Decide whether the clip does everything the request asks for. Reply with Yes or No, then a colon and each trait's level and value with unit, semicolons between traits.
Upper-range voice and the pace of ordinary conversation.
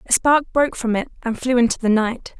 No: high, 240 Hz; fast, 250 wpm